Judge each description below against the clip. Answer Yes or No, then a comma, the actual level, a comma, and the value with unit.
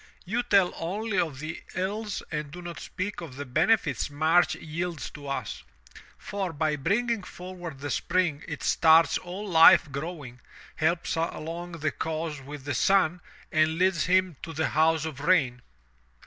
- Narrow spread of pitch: No, average, 3.3 semitones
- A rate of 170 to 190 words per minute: No, average, 160 wpm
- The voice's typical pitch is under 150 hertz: No, medium, 165 Hz